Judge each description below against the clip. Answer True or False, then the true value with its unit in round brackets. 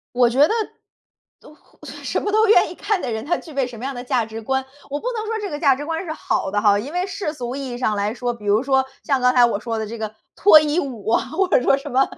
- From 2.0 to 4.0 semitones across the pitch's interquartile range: False (5.3 semitones)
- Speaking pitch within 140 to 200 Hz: False (265 Hz)